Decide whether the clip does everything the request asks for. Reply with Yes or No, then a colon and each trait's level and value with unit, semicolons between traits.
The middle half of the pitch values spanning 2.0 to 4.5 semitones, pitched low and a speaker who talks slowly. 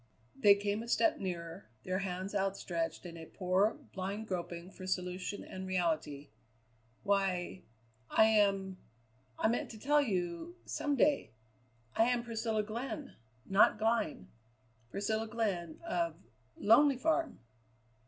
No: average, 3.9 semitones; high, 200 Hz; slow, 125 wpm